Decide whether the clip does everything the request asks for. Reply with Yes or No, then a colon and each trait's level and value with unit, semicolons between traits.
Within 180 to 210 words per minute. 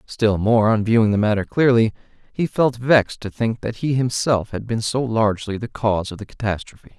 Yes: fast, 205 wpm